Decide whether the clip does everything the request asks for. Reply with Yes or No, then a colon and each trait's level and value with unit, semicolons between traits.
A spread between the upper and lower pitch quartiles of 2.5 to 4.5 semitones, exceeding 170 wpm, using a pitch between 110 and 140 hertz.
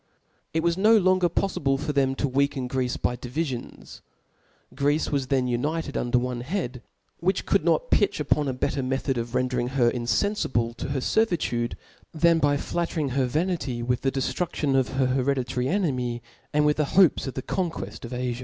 Yes: average, 4.2 semitones; average, 180 wpm; low, 135 Hz